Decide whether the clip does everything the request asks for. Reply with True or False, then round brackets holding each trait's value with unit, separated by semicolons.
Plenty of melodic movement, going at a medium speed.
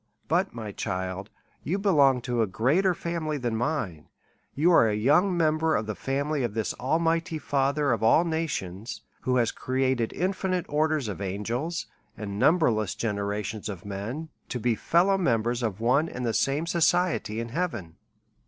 True (6.9 semitones; 170 wpm)